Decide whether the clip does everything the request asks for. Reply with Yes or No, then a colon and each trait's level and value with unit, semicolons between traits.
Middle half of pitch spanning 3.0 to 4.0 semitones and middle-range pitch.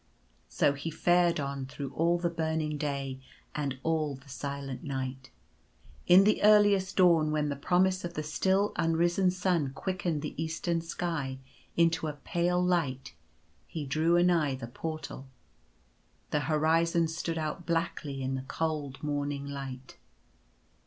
Yes: average, 3.5 semitones; medium, 155 Hz